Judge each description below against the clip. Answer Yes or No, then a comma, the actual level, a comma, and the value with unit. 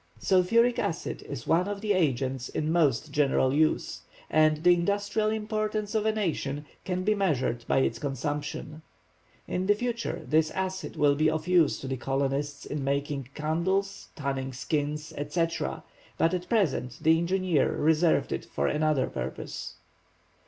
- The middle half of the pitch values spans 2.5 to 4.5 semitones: No, average, 5.0 semitones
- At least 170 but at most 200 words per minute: No, average, 150 wpm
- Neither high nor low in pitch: Yes, medium, 155 Hz